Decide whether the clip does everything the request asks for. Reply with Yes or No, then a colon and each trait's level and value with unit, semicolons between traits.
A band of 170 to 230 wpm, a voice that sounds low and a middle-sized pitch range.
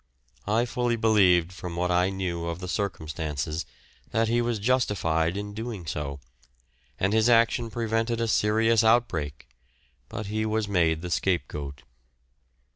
No: average, 140 wpm; low, 100 Hz; average, 5.0 semitones